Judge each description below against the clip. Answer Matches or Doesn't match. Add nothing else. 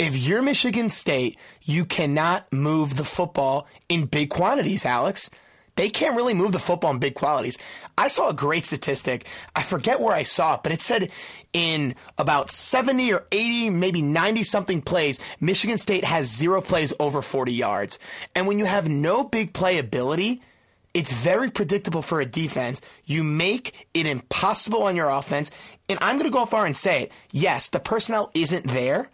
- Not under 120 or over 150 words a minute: Doesn't match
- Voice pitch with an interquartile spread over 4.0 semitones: Matches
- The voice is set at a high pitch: Doesn't match